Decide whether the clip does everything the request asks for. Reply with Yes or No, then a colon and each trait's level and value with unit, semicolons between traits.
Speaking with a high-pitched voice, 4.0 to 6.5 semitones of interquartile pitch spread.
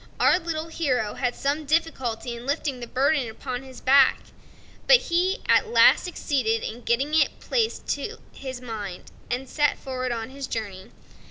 Yes: very high, 265 Hz; average, 4.5 semitones